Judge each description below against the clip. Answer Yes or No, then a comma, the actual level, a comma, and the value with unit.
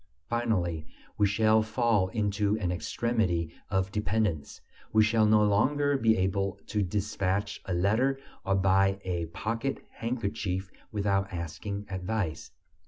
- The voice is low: Yes, low, 100 Hz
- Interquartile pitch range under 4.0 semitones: Yes, average, 2.8 semitones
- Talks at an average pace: No, slow, 125 wpm